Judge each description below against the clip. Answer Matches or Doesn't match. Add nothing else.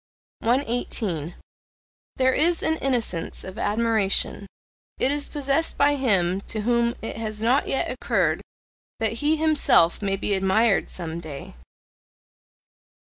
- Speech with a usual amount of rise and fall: Doesn't match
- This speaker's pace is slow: Matches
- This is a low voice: Doesn't match